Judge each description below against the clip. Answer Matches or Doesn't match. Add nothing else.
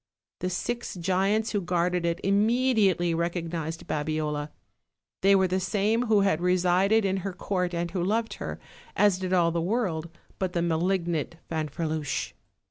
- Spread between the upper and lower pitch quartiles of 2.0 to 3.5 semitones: Matches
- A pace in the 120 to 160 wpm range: Matches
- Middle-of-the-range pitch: Matches